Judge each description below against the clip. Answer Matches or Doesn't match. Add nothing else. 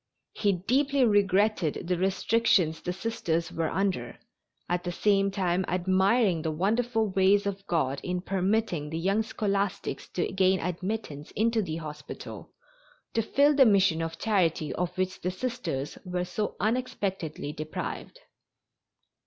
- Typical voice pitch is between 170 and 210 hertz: Matches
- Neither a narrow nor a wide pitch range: Matches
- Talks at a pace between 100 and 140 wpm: Matches